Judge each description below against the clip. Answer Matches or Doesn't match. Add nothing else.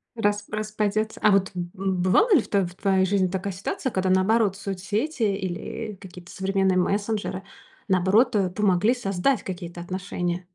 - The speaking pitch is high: Matches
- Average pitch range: Doesn't match